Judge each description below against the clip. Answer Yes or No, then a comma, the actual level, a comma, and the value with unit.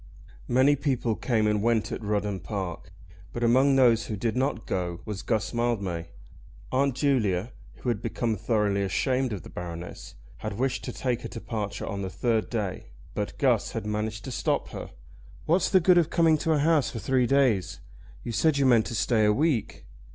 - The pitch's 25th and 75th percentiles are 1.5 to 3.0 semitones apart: No, average, 4.2 semitones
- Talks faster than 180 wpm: Yes, average, 190 wpm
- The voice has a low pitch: Yes, low, 115 Hz